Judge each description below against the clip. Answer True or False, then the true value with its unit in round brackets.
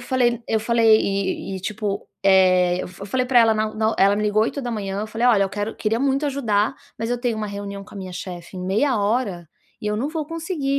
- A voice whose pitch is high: True (215 Hz)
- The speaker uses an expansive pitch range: False (3.5 semitones)